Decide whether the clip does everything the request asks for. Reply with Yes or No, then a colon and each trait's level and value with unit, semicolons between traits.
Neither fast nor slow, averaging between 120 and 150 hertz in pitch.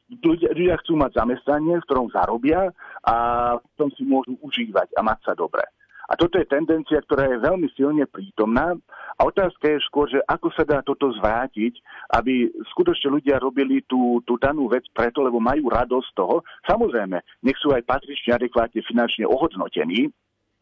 No: fast, 170 wpm; medium, 140 Hz